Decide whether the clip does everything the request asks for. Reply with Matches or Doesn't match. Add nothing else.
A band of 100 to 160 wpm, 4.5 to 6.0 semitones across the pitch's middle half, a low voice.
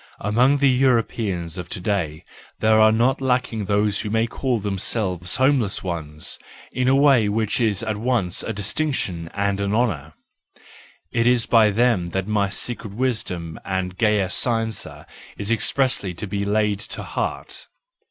Doesn't match